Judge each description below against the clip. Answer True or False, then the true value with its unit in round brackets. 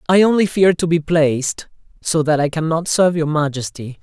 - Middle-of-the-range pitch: True (160 Hz)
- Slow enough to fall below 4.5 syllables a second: False (5.4 syllables/s)